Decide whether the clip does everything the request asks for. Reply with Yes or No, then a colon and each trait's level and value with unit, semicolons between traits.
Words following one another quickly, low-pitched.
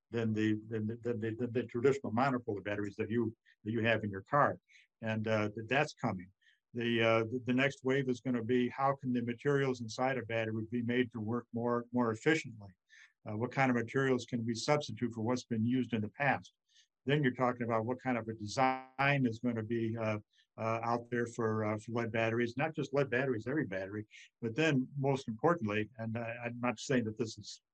Yes: fast, 225 wpm; low, 120 Hz